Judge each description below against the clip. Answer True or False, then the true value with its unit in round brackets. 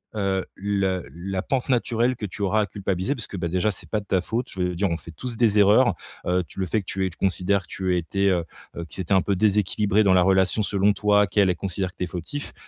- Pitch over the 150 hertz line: False (95 Hz)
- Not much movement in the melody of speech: True (2.3 semitones)